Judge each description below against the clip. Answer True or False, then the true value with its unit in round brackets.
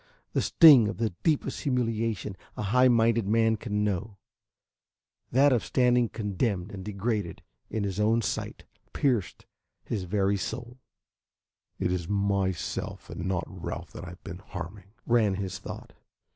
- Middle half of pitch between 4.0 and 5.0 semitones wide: False (3.4 semitones)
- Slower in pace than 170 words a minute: True (145 wpm)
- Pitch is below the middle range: True (105 Hz)